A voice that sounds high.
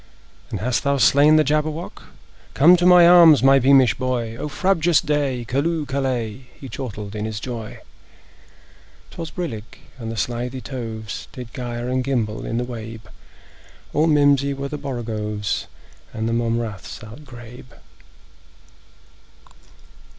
No: low, 125 Hz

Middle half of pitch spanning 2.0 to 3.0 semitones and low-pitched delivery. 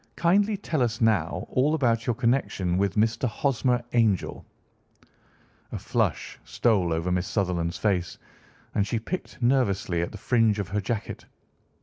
No: average, 4.3 semitones; low, 110 Hz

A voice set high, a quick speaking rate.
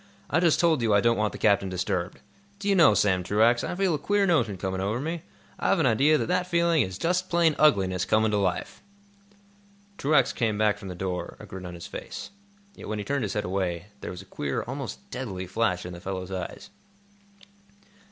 No: low, 110 Hz; fast, 215 wpm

